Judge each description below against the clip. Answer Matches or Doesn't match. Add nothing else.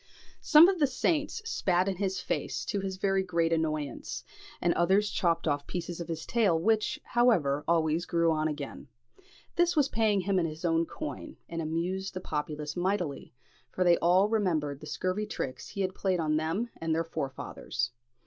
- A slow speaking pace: Doesn't match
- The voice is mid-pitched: Matches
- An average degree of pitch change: Matches